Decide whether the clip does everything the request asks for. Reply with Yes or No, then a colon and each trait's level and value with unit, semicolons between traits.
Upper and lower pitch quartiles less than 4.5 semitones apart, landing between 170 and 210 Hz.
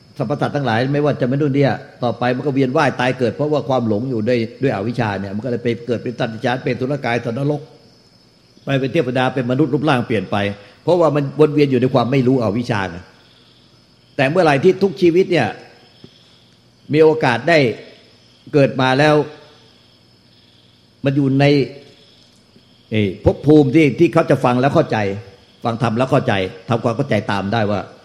No: average, 3.9 semitones; low, 130 Hz